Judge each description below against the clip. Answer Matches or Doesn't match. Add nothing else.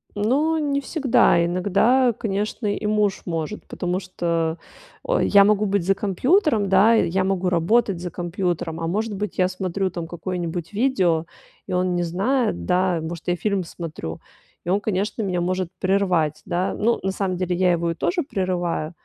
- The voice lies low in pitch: Doesn't match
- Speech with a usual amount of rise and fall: Matches